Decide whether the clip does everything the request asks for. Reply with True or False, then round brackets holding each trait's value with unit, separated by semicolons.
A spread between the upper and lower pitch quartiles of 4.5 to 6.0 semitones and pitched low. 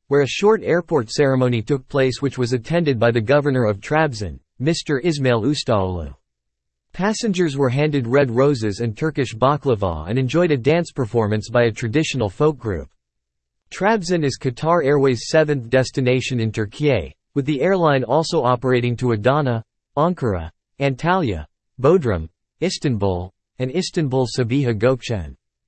True (5.1 semitones; 130 Hz)